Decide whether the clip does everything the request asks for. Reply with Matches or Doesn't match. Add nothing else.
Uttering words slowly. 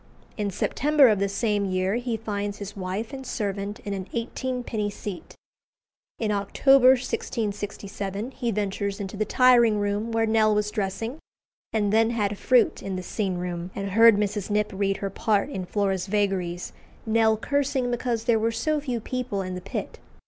Doesn't match